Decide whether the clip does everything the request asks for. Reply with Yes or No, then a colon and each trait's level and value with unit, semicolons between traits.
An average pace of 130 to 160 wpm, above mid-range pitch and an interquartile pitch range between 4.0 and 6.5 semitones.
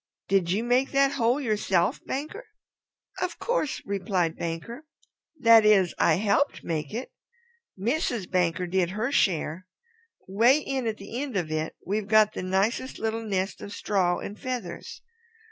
Yes: average, 150 wpm; high, 210 Hz; average, 5.0 semitones